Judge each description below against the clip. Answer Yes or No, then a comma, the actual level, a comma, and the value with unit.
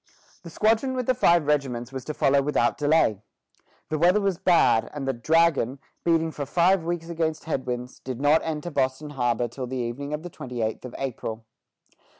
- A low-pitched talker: No, medium, 145 Hz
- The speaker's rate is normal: Yes, average, 185 wpm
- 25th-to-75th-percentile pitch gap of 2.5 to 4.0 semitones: No, average, 4.8 semitones